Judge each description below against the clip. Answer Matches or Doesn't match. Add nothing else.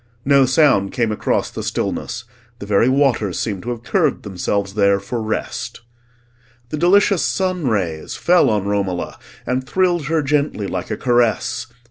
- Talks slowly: Doesn't match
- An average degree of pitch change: Doesn't match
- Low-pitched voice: Matches